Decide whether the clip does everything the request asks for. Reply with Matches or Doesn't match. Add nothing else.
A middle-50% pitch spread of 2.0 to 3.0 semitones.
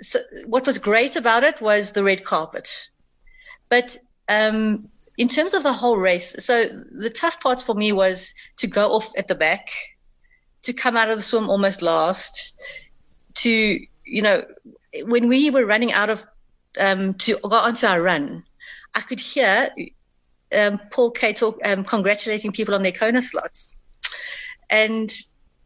Doesn't match